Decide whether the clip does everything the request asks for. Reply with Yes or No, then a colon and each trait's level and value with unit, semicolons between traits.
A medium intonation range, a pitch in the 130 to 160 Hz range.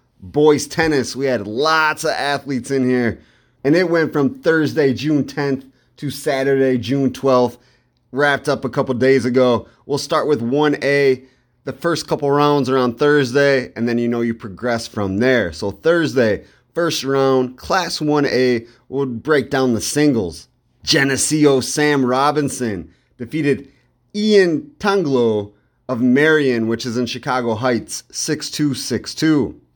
Yes: average, 3.2 semitones; low, 135 Hz